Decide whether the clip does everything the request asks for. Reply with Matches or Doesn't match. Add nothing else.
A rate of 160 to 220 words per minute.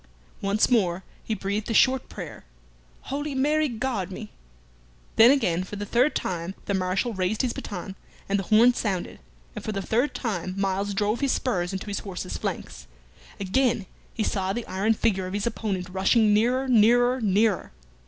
Matches